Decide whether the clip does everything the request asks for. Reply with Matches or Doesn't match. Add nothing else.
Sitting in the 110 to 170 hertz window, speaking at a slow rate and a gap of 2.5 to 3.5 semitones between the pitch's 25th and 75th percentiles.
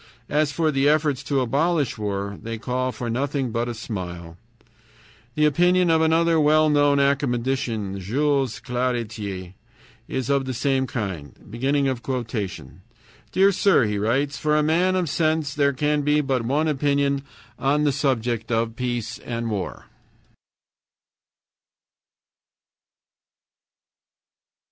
Doesn't match